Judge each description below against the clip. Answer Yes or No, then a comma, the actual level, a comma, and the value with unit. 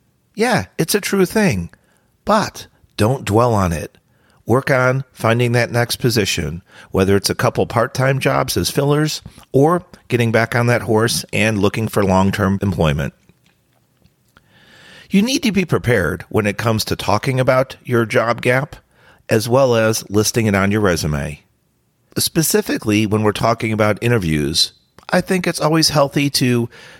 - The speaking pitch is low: Yes, low, 120 Hz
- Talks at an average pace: Yes, average, 160 wpm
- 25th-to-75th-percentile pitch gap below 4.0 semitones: No, average, 4.7 semitones